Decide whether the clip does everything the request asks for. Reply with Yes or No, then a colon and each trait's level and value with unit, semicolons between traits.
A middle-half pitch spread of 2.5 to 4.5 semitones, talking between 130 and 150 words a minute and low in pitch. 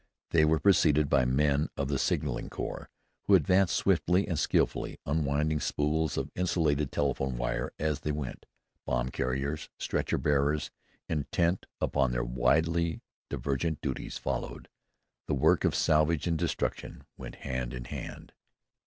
Yes: average, 2.9 semitones; average, 140 wpm; very low, 75 Hz